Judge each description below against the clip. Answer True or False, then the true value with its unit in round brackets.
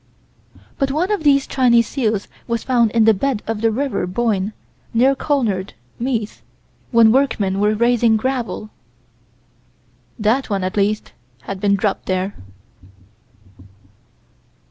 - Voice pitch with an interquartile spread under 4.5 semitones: True (3.9 semitones)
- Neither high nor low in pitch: False (225 Hz)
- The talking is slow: True (125 wpm)